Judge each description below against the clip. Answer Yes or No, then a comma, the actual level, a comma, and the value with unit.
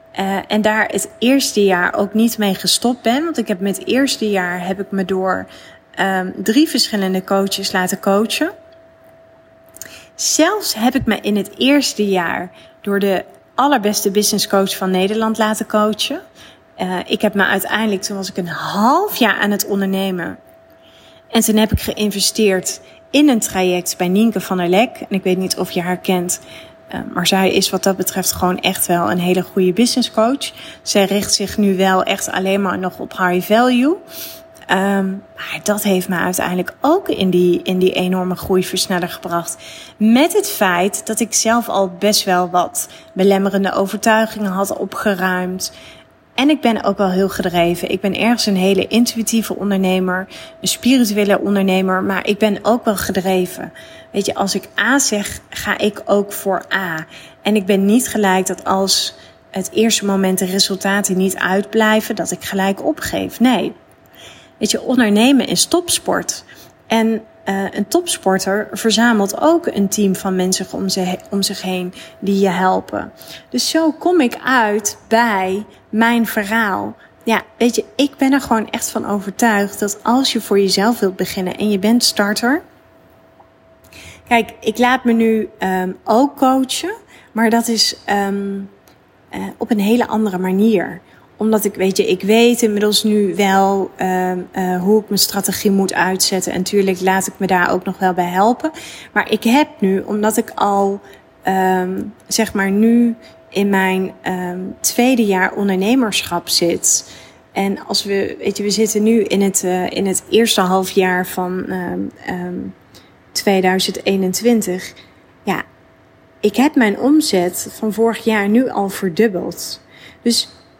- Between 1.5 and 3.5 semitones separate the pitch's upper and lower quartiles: Yes, average, 3.2 semitones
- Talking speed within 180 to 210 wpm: No, average, 165 wpm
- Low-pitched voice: No, high, 200 Hz